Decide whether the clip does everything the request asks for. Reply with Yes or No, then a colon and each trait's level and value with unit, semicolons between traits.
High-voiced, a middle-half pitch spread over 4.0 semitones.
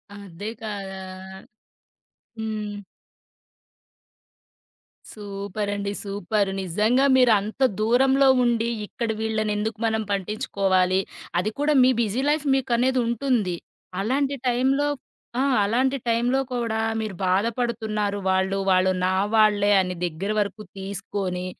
No: high, 215 Hz; average, 3.3 semitones